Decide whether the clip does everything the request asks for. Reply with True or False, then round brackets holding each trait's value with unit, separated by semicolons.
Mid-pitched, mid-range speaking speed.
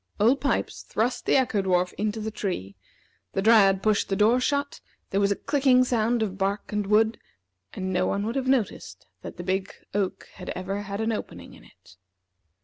False (210 Hz; 195 wpm)